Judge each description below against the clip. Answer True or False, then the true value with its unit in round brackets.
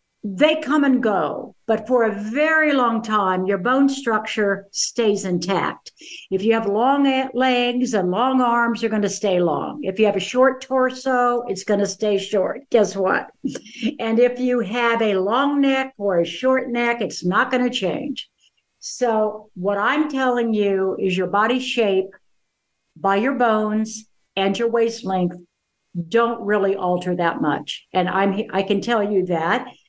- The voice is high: True (220 Hz)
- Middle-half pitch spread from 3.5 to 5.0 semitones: True (4.3 semitones)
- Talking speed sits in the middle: True (170 wpm)